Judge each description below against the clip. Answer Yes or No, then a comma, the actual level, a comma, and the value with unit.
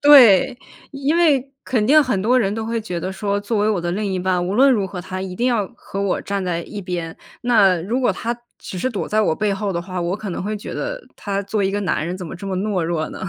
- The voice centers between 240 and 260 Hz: No, high, 200 Hz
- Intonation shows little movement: No, average, 3.8 semitones